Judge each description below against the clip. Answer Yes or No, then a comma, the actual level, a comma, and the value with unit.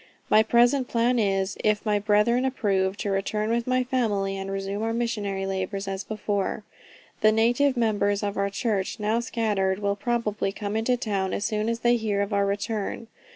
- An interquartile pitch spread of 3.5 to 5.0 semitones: No, average, 2.7 semitones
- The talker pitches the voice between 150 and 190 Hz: No, high, 210 Hz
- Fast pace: No, average, 185 wpm